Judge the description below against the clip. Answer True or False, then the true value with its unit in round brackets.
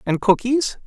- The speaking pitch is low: False (240 Hz)